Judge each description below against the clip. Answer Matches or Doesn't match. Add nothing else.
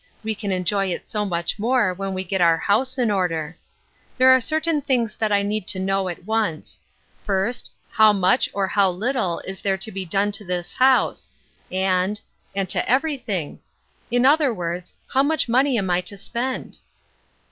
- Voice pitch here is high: Matches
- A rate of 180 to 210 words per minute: Matches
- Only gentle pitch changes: Doesn't match